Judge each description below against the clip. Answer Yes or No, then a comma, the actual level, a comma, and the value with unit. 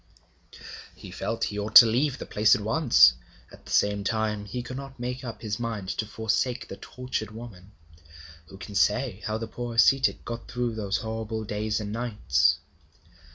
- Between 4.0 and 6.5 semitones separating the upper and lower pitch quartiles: No, narrow, 2.6 semitones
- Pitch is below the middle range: Yes, low, 110 Hz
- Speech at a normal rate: Yes, average, 180 wpm